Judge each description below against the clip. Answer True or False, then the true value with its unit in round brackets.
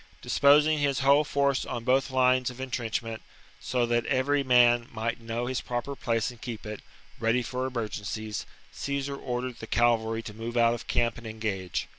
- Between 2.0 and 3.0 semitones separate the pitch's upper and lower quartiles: True (2.4 semitones)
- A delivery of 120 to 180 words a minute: False (190 wpm)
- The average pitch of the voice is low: True (120 Hz)